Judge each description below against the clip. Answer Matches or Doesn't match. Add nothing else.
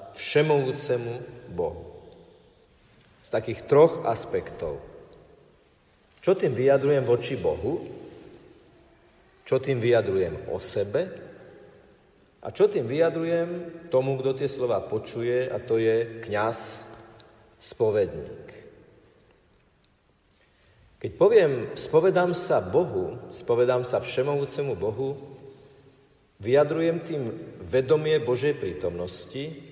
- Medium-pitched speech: Matches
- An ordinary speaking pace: Doesn't match